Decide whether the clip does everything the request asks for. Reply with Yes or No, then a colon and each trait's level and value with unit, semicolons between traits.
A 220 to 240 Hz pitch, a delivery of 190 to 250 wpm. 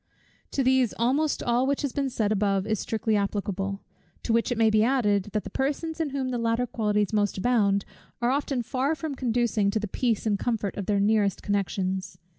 Yes: high, 225 Hz; fast, 205 wpm